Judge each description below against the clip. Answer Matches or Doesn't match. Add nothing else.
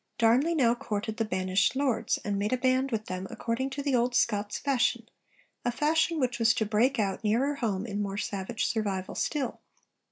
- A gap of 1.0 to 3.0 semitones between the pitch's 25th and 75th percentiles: Doesn't match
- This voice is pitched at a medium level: Doesn't match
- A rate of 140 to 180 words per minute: Doesn't match